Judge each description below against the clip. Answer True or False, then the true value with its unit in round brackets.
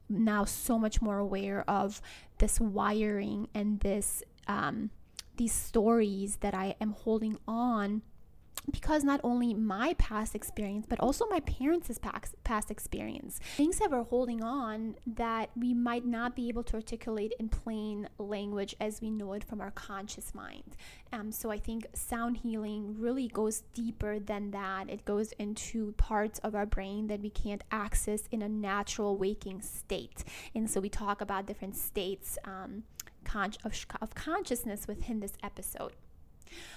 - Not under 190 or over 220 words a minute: False (160 wpm)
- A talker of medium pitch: False (215 Hz)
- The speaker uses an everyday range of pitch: False (2.3 semitones)